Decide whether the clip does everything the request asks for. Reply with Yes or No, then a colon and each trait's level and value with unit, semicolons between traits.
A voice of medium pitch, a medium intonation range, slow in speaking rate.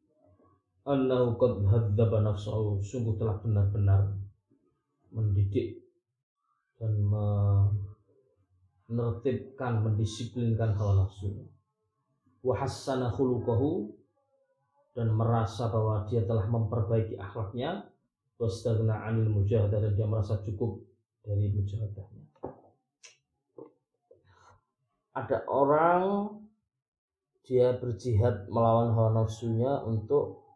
No: low, 115 Hz; average, 3.2 semitones; slow, 70 wpm